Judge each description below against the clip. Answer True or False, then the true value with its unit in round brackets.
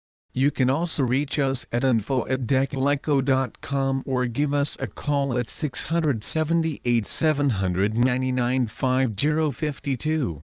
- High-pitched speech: False (135 Hz)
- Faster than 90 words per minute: False (85 wpm)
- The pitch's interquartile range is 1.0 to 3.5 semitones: True (2.6 semitones)